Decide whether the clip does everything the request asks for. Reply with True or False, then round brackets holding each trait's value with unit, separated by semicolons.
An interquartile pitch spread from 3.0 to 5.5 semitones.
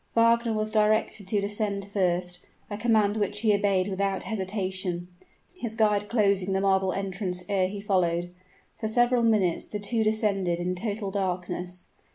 False (2.5 semitones)